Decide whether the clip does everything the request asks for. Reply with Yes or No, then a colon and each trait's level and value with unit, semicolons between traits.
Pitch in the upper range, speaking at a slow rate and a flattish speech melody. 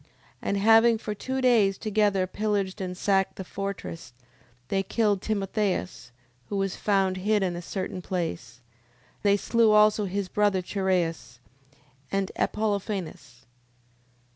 Yes: high, 195 Hz; slow, 130 wpm; narrow, 2.3 semitones